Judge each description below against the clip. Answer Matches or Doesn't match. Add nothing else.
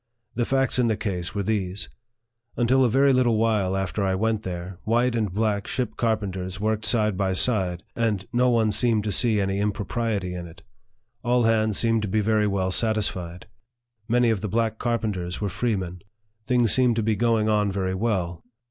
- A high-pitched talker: Doesn't match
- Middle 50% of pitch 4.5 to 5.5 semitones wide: Doesn't match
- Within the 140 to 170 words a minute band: Doesn't match